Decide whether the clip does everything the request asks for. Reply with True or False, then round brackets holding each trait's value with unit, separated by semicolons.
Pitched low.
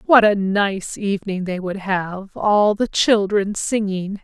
False (200 Hz)